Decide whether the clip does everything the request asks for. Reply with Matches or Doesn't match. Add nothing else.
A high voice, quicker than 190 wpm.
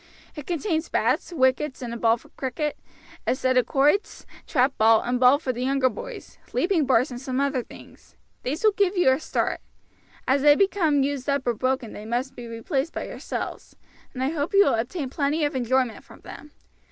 Matches